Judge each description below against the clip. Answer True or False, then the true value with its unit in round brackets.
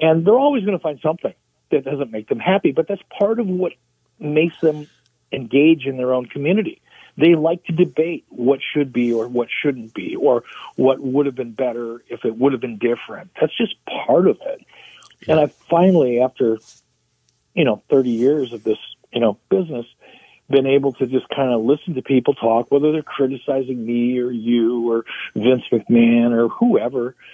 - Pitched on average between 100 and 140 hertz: True (135 Hz)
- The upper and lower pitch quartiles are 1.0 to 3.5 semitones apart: False (4.9 semitones)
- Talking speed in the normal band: True (190 wpm)